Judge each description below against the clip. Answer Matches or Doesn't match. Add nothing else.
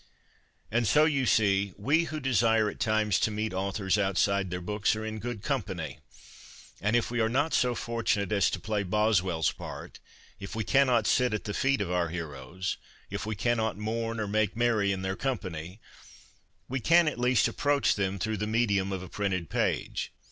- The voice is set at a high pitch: Doesn't match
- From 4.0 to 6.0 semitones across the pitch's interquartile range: Doesn't match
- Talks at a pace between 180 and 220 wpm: Matches